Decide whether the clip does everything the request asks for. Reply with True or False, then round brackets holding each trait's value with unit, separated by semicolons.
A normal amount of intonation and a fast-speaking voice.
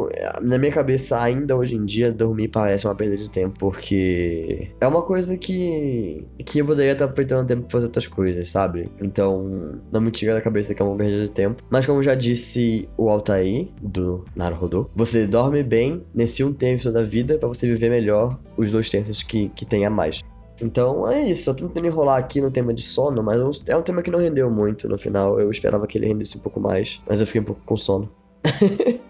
True (4.5 semitones; 220 wpm)